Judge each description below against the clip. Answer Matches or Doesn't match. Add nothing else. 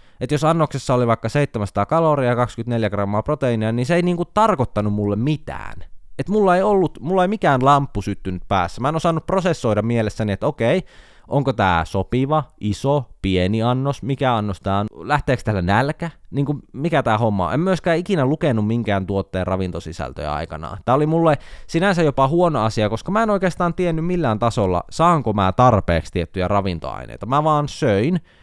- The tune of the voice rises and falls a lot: Matches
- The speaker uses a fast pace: Matches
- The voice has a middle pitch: Doesn't match